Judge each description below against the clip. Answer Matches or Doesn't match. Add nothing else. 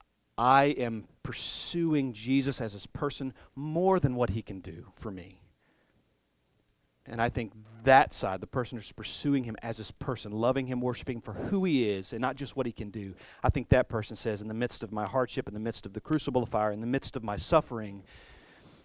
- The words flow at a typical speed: Doesn't match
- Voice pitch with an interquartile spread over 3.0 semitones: Matches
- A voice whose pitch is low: Matches